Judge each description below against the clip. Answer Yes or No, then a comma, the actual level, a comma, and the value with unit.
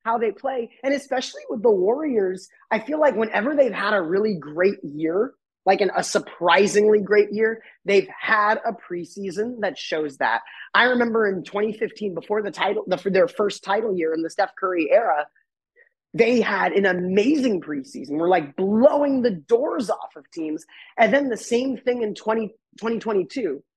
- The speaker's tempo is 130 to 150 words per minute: No, average, 175 wpm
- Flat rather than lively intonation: No, average, 4.5 semitones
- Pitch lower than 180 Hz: No, high, 215 Hz